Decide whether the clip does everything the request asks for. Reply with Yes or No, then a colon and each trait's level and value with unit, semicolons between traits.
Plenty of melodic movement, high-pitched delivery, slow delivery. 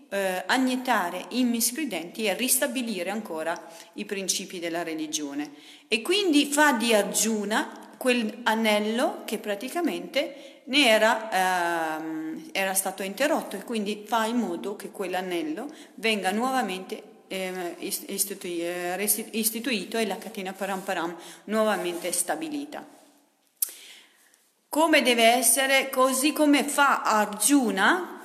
Yes: wide, 5.8 semitones; high, 220 Hz; slow, 110 wpm